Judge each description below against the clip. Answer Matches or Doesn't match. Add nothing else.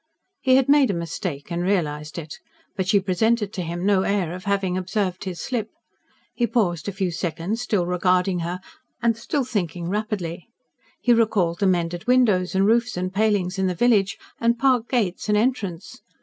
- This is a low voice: Doesn't match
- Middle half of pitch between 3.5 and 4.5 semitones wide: Matches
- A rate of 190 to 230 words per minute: Doesn't match